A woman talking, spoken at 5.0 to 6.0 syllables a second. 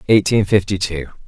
No: male; 5.3 syllables/s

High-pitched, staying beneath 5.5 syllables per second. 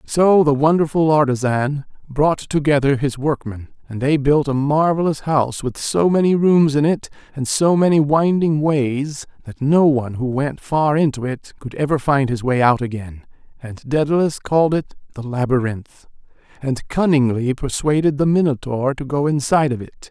No: medium, 140 Hz; 4.8 syllables/s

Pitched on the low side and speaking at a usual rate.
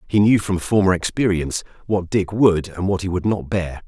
No: very low, 95 Hz; fast, 215 wpm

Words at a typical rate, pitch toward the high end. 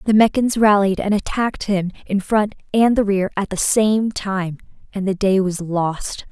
Yes: average, 190 wpm; high, 200 Hz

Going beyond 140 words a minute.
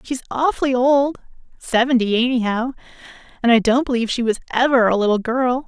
No: slow, 135 wpm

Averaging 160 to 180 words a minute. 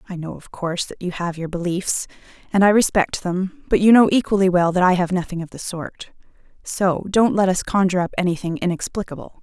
No: fast, 205 wpm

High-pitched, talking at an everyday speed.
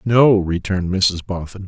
No: very low, 95 Hz; average, 145 wpm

